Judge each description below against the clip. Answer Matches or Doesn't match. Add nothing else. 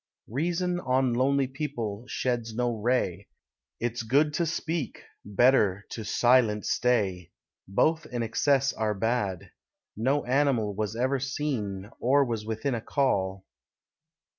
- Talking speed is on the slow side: Matches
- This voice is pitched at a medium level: Doesn't match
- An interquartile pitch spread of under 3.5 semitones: Doesn't match